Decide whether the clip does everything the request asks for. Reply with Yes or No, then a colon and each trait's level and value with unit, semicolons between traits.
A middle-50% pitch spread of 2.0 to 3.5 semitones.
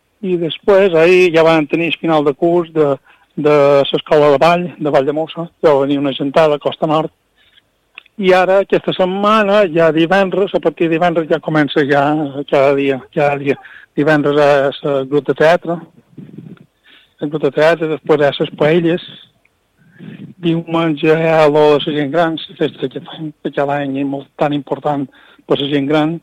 Yes: narrow, 2.6 semitones